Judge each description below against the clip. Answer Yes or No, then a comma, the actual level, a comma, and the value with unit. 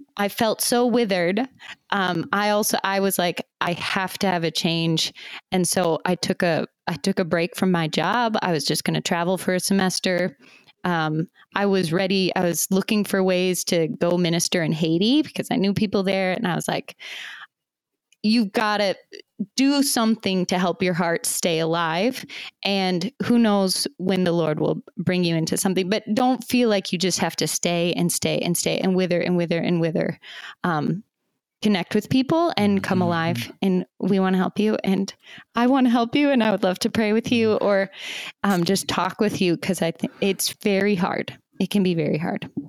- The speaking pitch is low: No, high, 190 Hz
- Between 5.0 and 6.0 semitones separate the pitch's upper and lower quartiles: No, average, 3.4 semitones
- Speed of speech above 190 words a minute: Yes, fast, 205 wpm